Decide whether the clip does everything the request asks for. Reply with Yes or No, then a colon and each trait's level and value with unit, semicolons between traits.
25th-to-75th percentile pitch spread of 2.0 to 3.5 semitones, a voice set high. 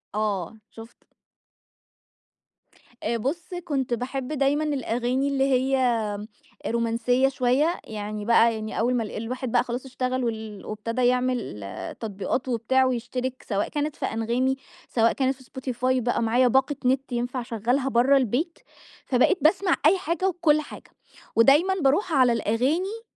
Yes: average, 2.9 semitones; very high, 255 Hz